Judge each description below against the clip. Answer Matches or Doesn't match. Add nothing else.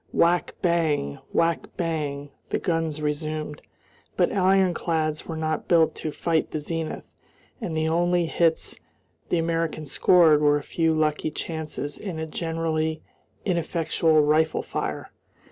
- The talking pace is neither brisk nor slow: Doesn't match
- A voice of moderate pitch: Matches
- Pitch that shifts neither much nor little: Doesn't match